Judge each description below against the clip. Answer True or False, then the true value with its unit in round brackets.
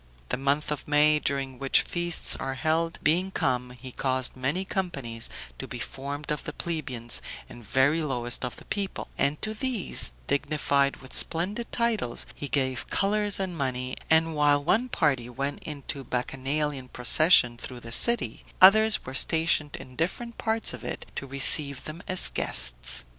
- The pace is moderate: True (165 wpm)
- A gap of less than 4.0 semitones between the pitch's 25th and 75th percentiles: False (4.7 semitones)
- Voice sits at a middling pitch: True (145 Hz)